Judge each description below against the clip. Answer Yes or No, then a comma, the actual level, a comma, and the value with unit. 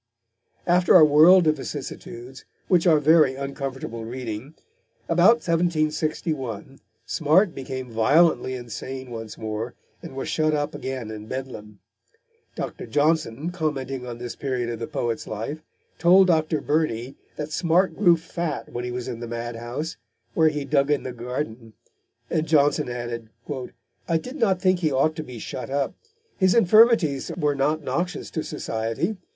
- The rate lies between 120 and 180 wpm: Yes, average, 150 wpm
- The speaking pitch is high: No, medium, 140 Hz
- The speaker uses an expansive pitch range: No, average, 4.9 semitones